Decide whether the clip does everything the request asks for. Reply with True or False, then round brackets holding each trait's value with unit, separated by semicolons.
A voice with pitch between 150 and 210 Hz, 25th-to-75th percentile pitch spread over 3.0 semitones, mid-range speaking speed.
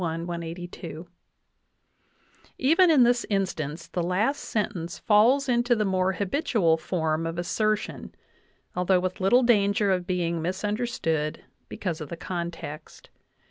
False (185 Hz; 4.2 semitones; 120 wpm)